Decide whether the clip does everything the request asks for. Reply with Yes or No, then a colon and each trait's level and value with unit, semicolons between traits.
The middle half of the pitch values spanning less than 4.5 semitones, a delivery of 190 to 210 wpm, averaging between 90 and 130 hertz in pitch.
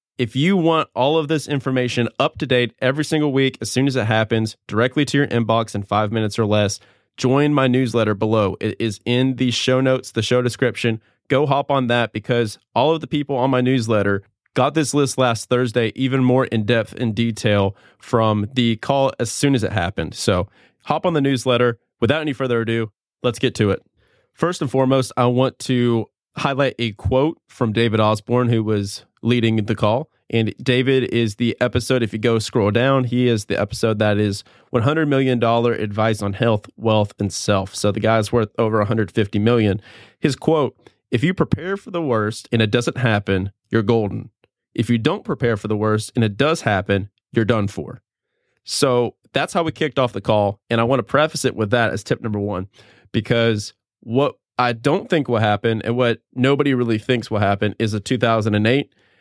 Yes: average, 3.3 semitones; average, 200 wpm; low, 120 Hz